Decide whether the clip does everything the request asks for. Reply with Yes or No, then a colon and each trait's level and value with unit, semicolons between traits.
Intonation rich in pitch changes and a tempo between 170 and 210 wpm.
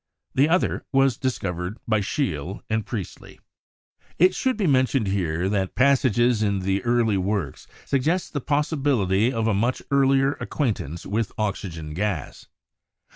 No: wide, 5.8 semitones; slow, 135 wpm